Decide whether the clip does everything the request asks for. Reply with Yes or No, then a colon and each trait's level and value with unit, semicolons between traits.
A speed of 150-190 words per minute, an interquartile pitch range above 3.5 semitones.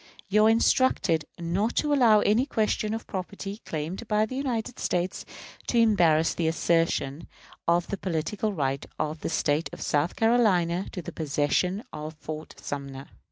Yes: average, 160 wpm; wide, 5.6 semitones